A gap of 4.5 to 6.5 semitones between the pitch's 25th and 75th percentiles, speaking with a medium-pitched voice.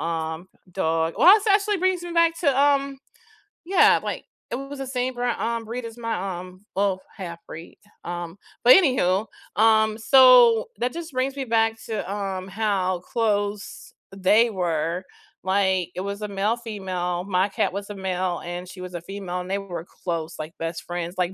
No: average, 5.1 semitones; high, 200 Hz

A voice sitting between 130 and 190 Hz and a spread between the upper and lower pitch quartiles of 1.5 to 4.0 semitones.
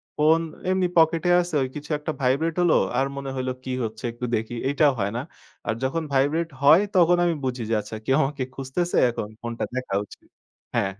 No: low, 135 Hz; average, 4.5 semitones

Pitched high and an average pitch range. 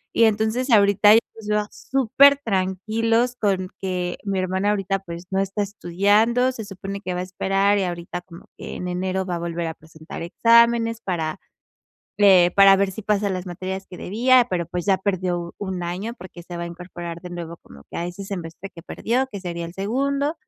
Yes: high, 195 Hz; average, 3.4 semitones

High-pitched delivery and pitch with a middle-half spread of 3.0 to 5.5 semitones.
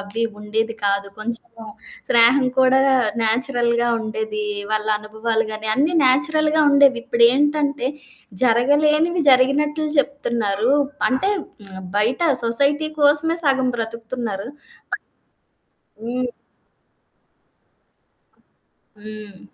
Yes: high, 240 Hz; average, 4.2 semitones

